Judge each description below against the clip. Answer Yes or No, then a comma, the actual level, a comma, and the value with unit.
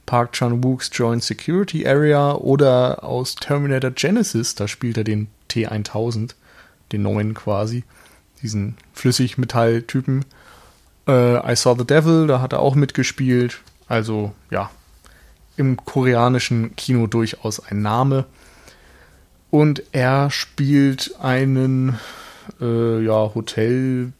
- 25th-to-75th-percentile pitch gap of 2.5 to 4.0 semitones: Yes, average, 3.3 semitones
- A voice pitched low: Yes, low, 125 Hz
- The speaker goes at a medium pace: No, slow, 110 wpm